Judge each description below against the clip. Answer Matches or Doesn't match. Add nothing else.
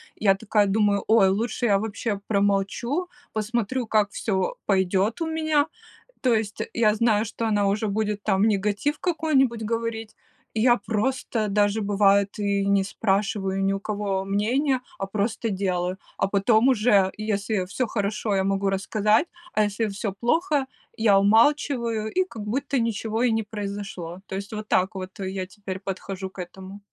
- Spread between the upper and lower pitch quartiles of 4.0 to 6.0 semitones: Doesn't match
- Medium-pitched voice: Doesn't match